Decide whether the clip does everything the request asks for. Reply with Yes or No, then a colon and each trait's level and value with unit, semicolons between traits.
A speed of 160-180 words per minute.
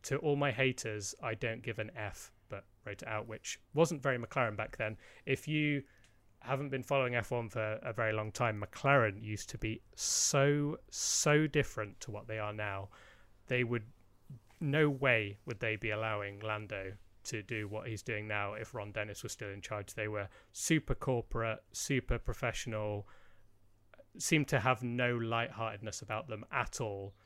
Yes: average, 175 wpm